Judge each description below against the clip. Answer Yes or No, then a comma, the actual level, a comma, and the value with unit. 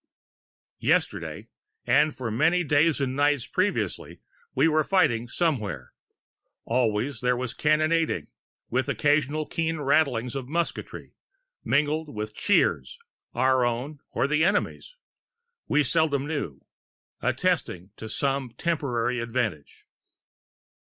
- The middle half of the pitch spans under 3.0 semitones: No, average, 4.3 semitones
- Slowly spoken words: Yes, slow, 105 wpm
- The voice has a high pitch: No, medium, 140 Hz